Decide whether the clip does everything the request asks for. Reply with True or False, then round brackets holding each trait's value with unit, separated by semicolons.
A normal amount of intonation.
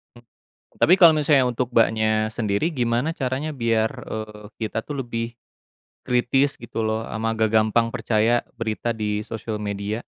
False (2.2 semitones)